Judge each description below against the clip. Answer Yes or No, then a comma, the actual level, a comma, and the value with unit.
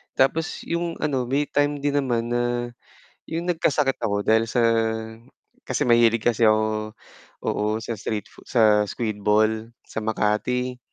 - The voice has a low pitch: Yes, low, 120 Hz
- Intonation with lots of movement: No, average, 3.5 semitones